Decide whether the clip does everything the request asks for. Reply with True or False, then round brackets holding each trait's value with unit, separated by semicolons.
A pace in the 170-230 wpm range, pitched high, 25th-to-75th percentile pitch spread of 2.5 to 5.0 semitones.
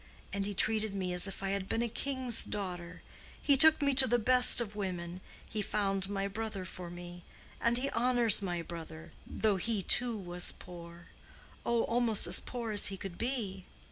True (180 wpm; 200 Hz; 4.4 semitones)